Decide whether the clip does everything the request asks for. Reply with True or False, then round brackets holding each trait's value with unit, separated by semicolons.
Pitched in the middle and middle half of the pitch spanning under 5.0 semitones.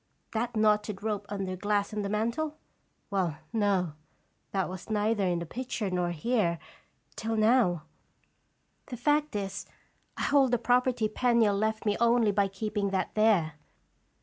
False (210 Hz; 3.1 semitones)